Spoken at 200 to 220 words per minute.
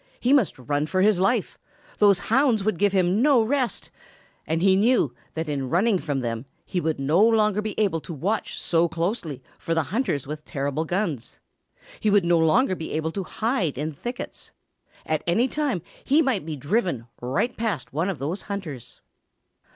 No: average, 180 wpm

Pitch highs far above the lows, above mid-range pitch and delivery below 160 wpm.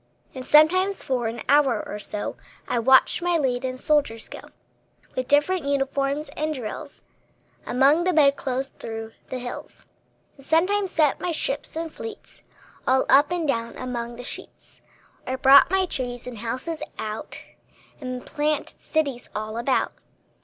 No: average, 3.9 semitones; very high, 275 Hz; average, 150 wpm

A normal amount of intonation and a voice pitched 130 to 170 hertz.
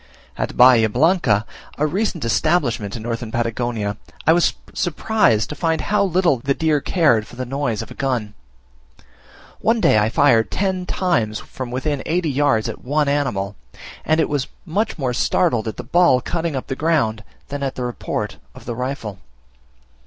No: wide, 5.9 semitones; low, 135 Hz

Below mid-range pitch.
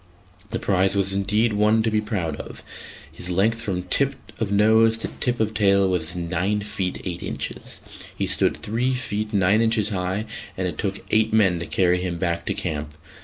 Yes: low, 100 Hz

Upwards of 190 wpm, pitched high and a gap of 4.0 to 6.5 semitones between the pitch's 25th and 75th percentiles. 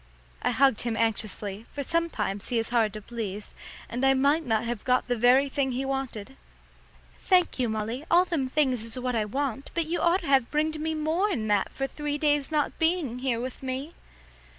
Yes: average, 200 wpm; very high, 265 Hz; average, 4.7 semitones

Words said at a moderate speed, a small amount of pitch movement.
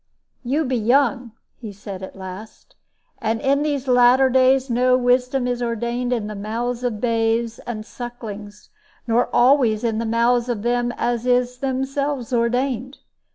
Yes: average, 155 wpm; narrow, 2.0 semitones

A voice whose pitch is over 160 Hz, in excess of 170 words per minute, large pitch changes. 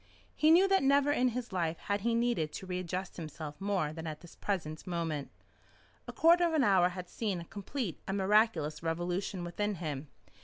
Yes: medium, 185 Hz; average, 190 wpm; wide, 5.9 semitones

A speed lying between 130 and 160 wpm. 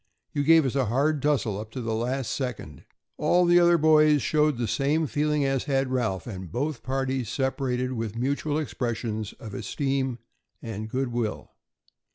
No: average, 170 wpm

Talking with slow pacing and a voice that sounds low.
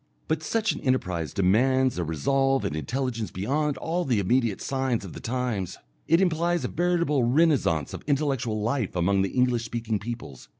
No: average, 170 wpm; low, 125 Hz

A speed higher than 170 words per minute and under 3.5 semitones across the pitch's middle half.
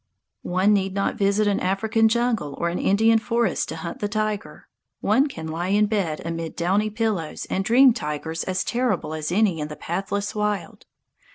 No: average, 180 wpm; average, 4.2 semitones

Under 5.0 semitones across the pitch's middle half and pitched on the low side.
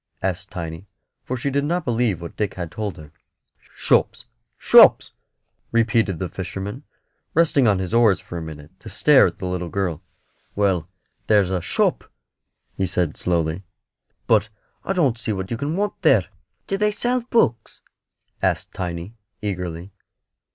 No: wide, 5.5 semitones; low, 100 Hz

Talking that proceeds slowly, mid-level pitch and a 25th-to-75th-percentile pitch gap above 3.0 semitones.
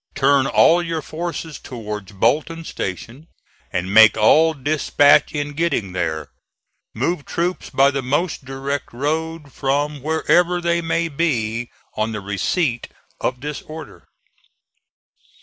Yes: slow, 125 wpm; medium, 145 Hz; wide, 5.6 semitones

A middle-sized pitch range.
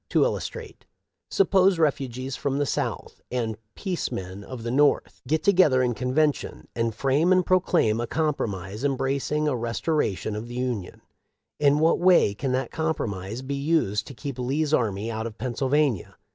Yes: average, 4.9 semitones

